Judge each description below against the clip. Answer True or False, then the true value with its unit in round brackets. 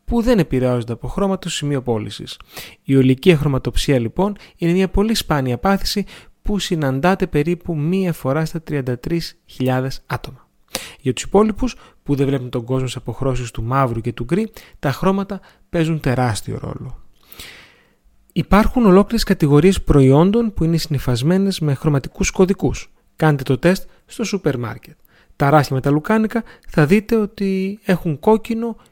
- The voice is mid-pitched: True (160 Hz)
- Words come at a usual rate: True (145 wpm)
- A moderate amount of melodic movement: False (6.5 semitones)